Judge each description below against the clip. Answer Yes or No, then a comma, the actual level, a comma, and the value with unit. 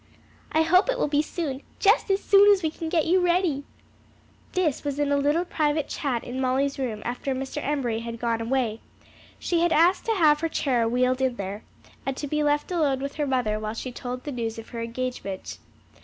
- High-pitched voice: Yes, very high, 280 Hz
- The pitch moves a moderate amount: Yes, average, 4.6 semitones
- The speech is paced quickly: Yes, fast, 215 wpm